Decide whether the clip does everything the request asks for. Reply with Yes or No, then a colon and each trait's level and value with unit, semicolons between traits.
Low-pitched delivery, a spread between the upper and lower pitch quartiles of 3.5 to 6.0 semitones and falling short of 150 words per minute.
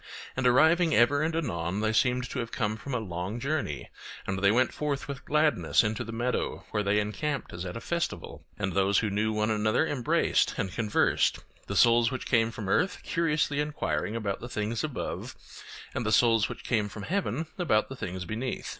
No: low, 115 Hz; average, 5.1 semitones; average, 200 wpm